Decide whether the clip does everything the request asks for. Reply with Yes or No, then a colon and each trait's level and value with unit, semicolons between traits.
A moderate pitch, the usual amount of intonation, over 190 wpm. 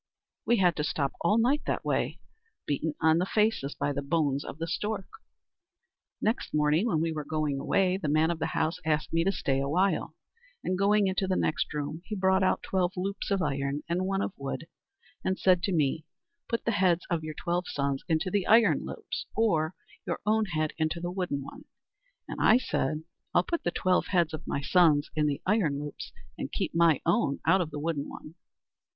Yes: medium, 170 Hz; average, 4.0 semitones; fast, 205 wpm